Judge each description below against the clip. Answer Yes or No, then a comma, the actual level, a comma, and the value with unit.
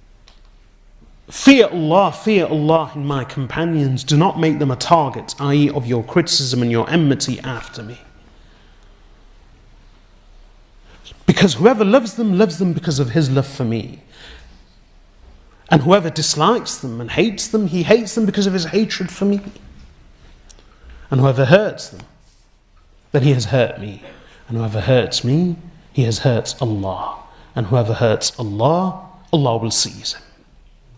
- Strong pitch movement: Yes, wide, 7.7 semitones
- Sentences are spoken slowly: No, average, 145 wpm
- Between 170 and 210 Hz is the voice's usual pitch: No, low, 135 Hz